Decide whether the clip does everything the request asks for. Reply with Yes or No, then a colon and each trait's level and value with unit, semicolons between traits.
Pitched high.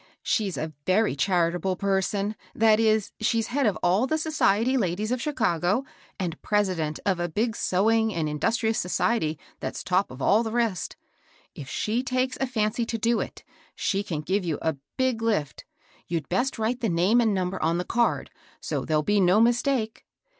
Yes: high, 210 Hz